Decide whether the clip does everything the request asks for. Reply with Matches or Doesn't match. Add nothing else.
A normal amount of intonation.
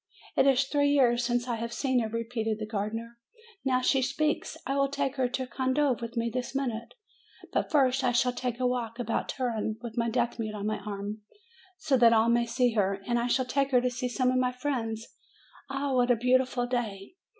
Doesn't match